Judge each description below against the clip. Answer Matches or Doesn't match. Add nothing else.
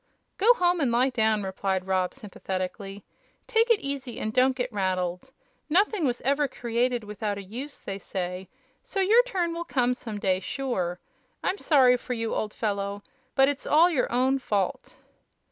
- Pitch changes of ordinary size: Doesn't match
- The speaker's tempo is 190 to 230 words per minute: Doesn't match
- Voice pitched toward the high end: Matches